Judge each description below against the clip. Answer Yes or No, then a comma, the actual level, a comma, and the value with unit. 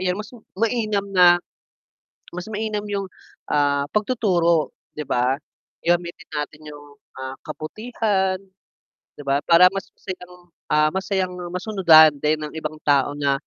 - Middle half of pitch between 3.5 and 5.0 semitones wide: Yes, average, 4.6 semitones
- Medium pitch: Yes, medium, 175 Hz